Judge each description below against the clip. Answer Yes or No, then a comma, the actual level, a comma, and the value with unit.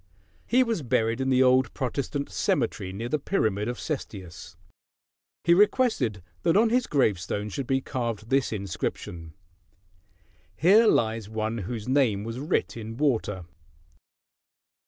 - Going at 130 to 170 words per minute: Yes, slow, 135 wpm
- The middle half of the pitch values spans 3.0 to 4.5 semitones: No, average, 5.3 semitones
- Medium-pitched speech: No, low, 120 Hz